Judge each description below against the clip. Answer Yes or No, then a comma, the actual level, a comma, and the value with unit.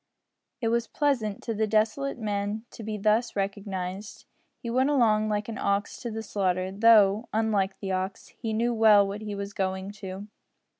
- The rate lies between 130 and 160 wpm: No, average, 180 wpm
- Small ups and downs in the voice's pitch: Yes, narrow, 2.1 semitones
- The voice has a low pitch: No, high, 210 Hz